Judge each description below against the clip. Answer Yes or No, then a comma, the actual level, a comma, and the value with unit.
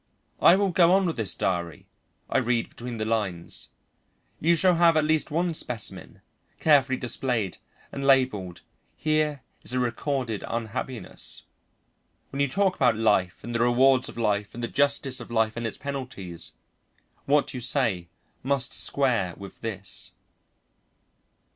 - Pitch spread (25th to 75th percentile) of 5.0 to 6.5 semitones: No, average, 4.3 semitones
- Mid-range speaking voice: No, low, 125 Hz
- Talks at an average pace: Yes, average, 150 wpm